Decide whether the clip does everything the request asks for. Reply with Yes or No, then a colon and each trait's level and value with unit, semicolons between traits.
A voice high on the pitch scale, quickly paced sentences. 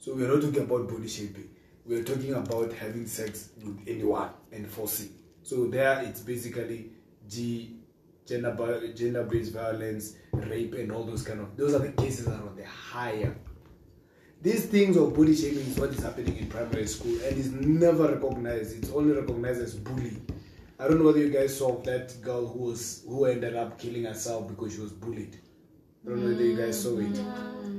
No: low, 115 Hz; fast, 190 wpm